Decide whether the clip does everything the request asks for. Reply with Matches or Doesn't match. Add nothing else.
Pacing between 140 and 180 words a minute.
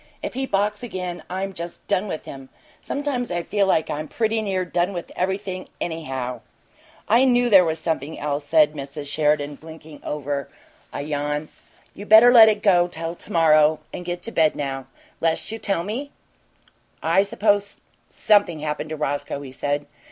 Matches